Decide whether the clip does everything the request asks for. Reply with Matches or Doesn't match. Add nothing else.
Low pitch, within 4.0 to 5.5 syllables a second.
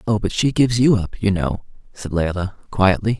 Matches